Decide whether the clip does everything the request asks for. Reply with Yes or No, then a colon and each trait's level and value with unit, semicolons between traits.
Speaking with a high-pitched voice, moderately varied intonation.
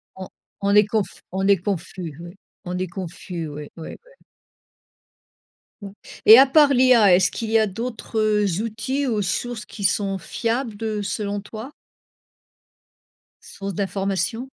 Yes: high, 205 Hz; average, 3.1 semitones